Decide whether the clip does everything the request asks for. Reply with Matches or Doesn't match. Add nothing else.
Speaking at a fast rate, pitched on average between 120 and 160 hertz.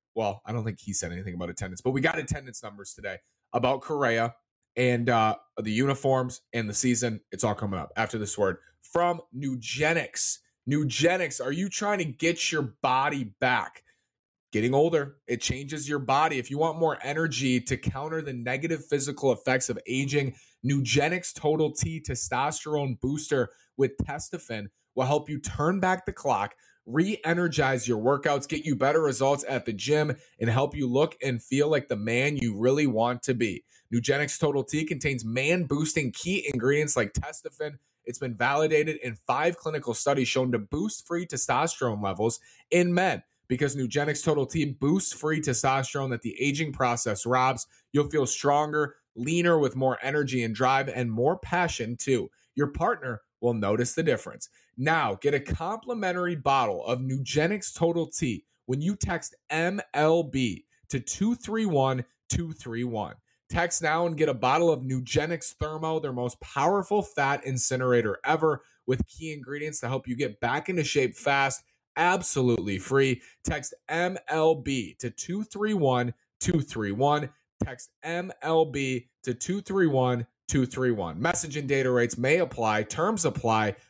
Doesn't match